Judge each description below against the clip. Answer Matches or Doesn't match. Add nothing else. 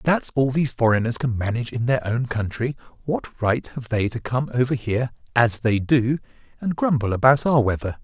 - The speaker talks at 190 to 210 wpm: Matches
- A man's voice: Matches